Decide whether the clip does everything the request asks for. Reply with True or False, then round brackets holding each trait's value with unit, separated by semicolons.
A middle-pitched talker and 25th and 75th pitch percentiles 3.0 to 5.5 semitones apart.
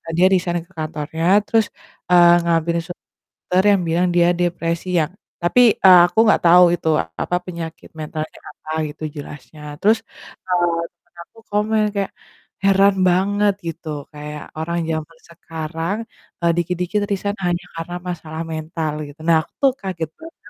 False (170 Hz; 2.5 semitones)